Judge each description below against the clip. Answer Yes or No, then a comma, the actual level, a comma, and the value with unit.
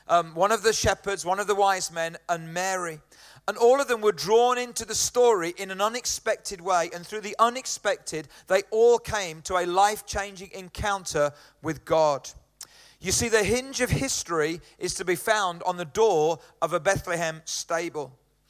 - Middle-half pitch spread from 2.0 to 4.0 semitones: No, average, 4.5 semitones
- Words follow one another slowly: No, average, 180 wpm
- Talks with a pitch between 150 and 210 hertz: Yes, high, 190 Hz